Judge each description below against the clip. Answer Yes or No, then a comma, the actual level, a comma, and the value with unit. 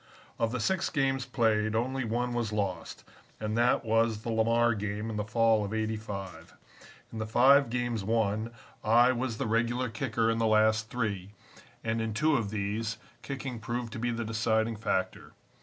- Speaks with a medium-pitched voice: No, low, 115 Hz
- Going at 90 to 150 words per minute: No, average, 175 wpm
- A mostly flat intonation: Yes, narrow, 1.9 semitones